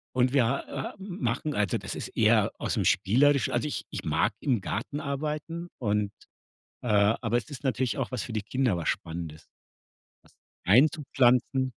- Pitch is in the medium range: No, low, 125 Hz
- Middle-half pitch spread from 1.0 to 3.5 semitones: No, average, 4.2 semitones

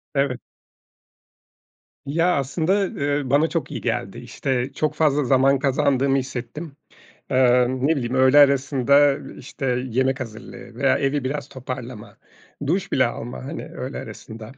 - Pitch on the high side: No, low, 135 Hz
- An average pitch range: No, narrow, 2.2 semitones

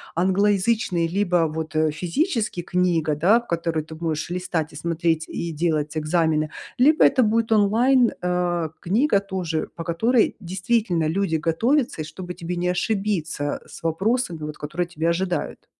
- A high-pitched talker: No, medium, 175 Hz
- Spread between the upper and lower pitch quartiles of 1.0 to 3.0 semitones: No, average, 4.1 semitones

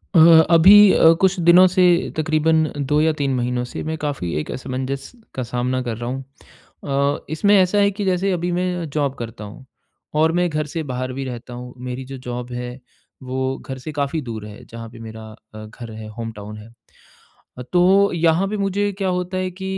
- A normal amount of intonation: No, wide, 6.3 semitones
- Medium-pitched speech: Yes, medium, 145 Hz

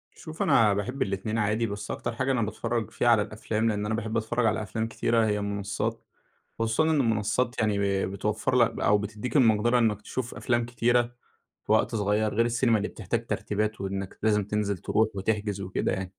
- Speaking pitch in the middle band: No, low, 110 Hz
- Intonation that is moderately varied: No, narrow, 2.2 semitones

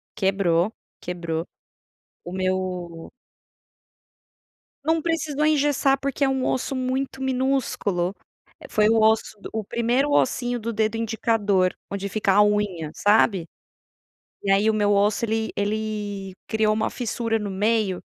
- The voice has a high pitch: Yes, high, 215 Hz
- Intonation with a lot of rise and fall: No, average, 3.9 semitones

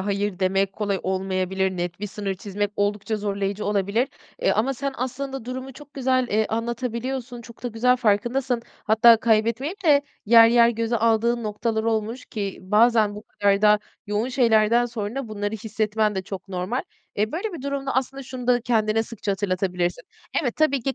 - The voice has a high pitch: Yes, high, 225 Hz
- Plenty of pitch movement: No, average, 3.3 semitones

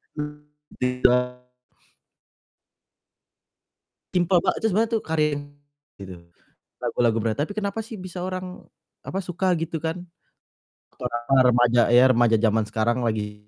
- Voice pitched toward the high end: No, medium, 150 Hz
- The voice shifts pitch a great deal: Yes, wide, 7.3 semitones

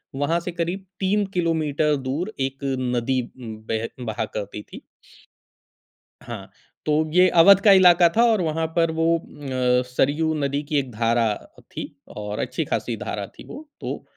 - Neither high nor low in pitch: Yes, medium, 155 Hz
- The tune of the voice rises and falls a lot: Yes, wide, 5.7 semitones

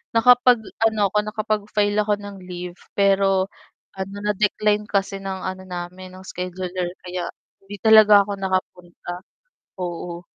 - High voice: Yes, high, 195 Hz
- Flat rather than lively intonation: Yes, narrow, 2.3 semitones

